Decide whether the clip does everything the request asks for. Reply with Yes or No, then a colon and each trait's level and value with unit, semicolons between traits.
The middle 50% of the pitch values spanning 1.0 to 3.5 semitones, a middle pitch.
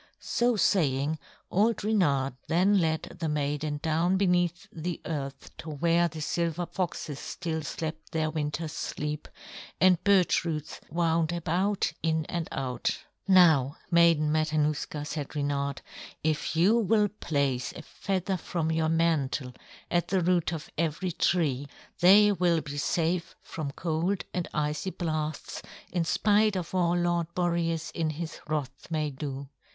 Yes: average, 2.8 semitones; medium, 165 Hz